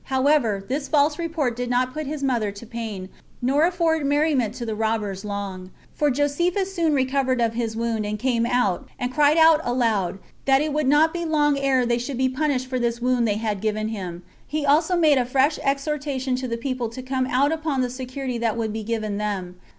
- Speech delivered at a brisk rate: Yes, fast, 210 wpm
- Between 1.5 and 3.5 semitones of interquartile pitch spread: No, average, 4.4 semitones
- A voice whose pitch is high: Yes, very high, 255 Hz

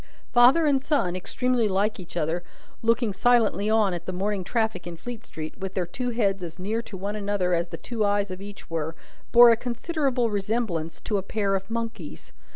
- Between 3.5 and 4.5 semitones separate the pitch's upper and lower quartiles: Yes, average, 4.2 semitones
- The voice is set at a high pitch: Yes, high, 205 Hz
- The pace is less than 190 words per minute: No, average, 200 wpm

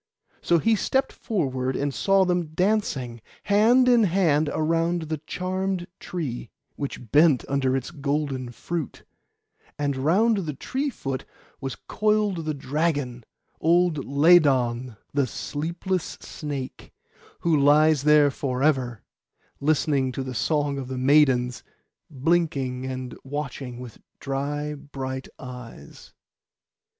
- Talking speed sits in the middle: No, slow, 120 wpm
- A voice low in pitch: No, medium, 145 Hz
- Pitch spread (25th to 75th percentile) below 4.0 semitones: No, average, 4.5 semitones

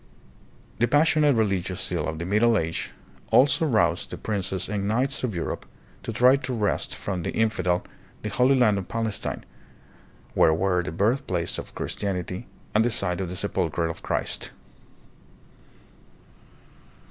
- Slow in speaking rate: No, average, 150 wpm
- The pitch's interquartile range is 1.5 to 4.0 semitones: No, average, 4.7 semitones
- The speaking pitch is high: No, low, 100 Hz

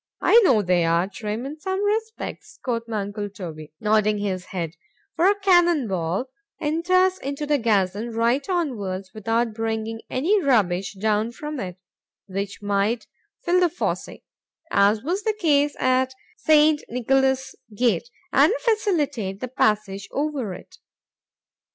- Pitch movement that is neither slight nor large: No, wide, 7.0 semitones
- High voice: Yes, high, 235 Hz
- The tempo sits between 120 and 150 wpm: Yes, slow, 135 wpm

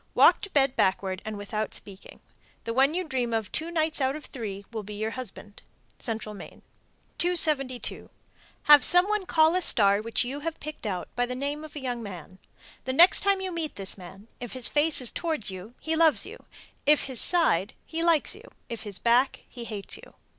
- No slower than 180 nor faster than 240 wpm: Yes, fast, 205 wpm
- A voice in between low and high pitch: No, very high, 255 Hz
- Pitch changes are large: Yes, wide, 6.8 semitones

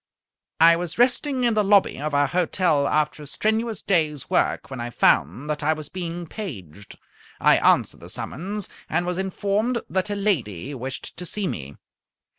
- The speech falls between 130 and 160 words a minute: No, average, 175 wpm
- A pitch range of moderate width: No, wide, 6.1 semitones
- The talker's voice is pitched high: No, medium, 170 Hz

